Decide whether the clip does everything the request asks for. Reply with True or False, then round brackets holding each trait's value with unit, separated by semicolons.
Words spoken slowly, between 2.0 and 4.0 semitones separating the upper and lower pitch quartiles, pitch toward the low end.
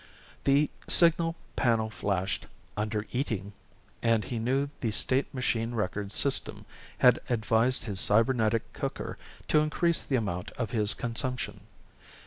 True (125 wpm; 3.7 semitones; 115 Hz)